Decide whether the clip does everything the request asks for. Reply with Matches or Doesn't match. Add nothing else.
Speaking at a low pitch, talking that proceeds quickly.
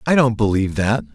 Matches